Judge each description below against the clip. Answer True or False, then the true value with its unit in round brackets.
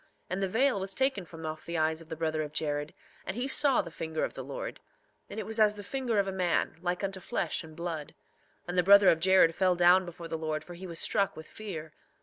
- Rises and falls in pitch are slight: False (3.6 semitones)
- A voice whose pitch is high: False (180 Hz)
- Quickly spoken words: True (255 wpm)